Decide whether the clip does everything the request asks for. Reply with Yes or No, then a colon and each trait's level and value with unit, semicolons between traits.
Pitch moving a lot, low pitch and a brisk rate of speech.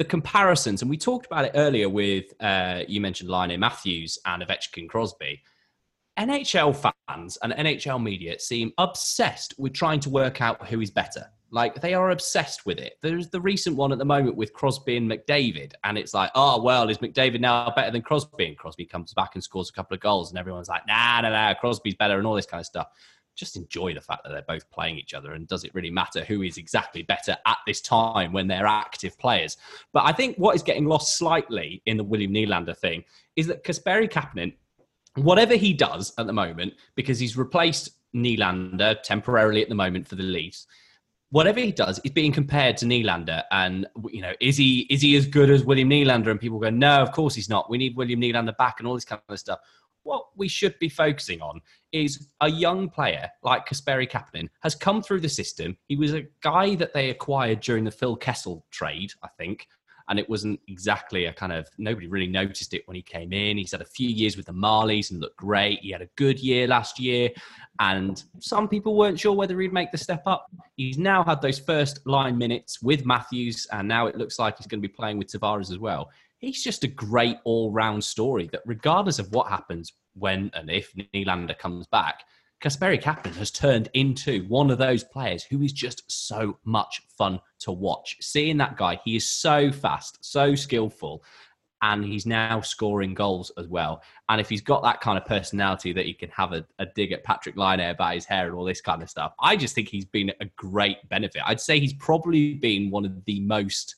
Yes: wide, 6.1 semitones; low, 115 Hz; fast, 220 wpm